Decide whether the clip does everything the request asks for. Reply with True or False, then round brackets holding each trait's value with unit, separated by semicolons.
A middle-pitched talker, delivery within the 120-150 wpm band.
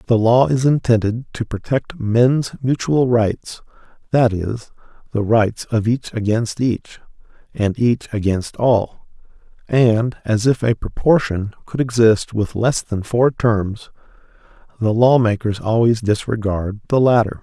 False (115 Hz; 135 wpm)